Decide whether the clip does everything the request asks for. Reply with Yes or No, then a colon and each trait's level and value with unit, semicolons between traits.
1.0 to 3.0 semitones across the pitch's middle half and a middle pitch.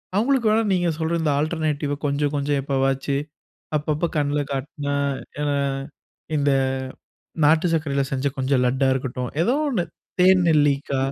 Yes: narrow, 2.6 semitones; medium, 145 Hz